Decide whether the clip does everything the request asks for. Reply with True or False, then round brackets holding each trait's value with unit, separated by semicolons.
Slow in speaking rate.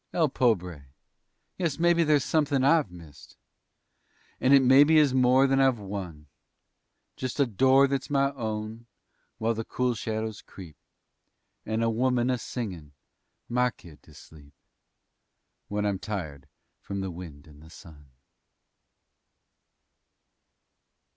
True (130 wpm)